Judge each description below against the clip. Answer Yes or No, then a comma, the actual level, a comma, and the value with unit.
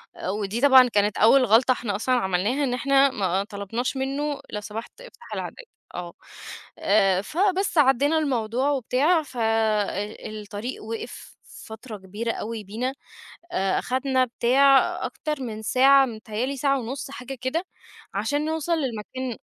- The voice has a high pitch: Yes, very high, 250 Hz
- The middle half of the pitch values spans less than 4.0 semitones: No, average, 4.3 semitones